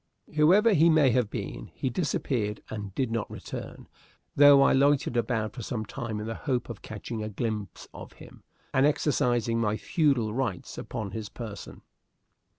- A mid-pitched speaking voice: No, low, 120 Hz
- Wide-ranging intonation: No, average, 4.4 semitones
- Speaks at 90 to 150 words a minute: No, average, 165 wpm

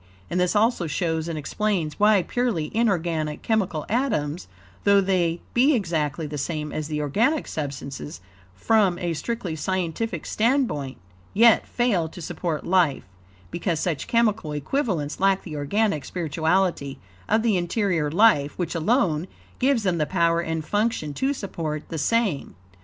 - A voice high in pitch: No, medium, 175 Hz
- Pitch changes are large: Yes, wide, 5.8 semitones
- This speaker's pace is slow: No, average, 145 wpm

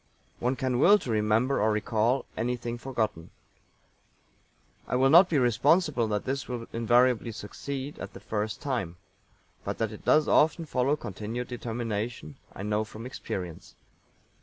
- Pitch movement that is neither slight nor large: Yes, average, 3.7 semitones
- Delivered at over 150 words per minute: No, average, 145 wpm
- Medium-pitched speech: No, low, 120 Hz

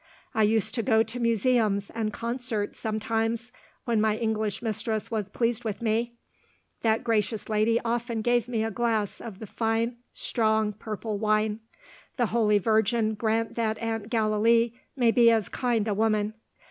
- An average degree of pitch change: No, narrow, 1.4 semitones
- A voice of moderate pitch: No, high, 225 Hz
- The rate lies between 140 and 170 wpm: Yes, average, 160 wpm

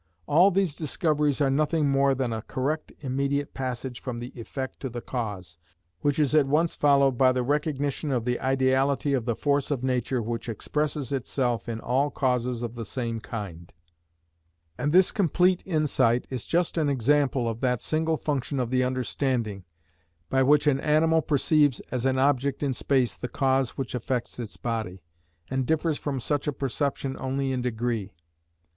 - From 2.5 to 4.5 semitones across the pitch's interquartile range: Yes, average, 3.0 semitones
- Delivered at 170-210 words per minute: Yes, average, 175 wpm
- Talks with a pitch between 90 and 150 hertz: Yes, low, 135 Hz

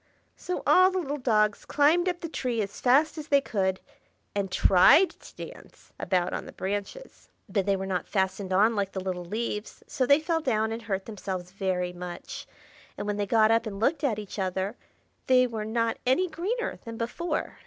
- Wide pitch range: Yes, wide, 6.4 semitones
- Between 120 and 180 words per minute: No, average, 195 wpm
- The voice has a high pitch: Yes, high, 220 Hz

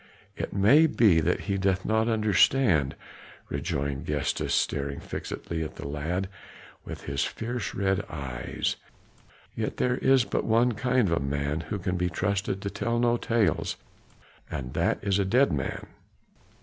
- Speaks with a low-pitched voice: Yes, very low, 95 Hz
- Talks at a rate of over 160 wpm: No, average, 155 wpm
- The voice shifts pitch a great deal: Yes, wide, 7.0 semitones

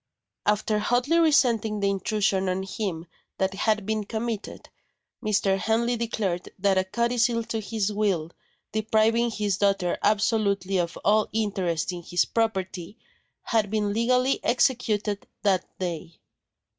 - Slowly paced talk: Yes, slow, 130 wpm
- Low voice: No, high, 210 Hz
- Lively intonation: No, average, 2.8 semitones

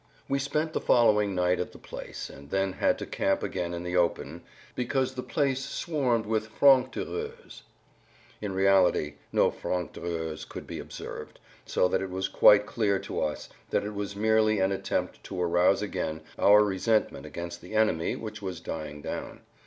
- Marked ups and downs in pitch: No, average, 3.7 semitones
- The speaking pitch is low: Yes, low, 100 Hz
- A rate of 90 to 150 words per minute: No, average, 175 wpm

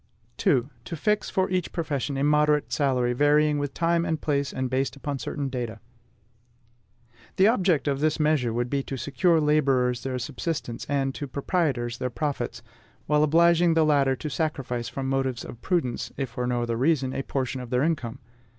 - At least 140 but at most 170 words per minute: No, average, 185 wpm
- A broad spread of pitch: No, average, 3.3 semitones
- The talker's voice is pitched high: No, medium, 140 Hz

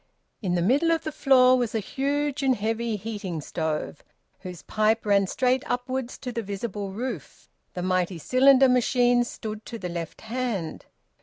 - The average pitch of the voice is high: Yes, high, 225 Hz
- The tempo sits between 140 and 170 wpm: Yes, average, 165 wpm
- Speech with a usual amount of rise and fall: Yes, average, 4.9 semitones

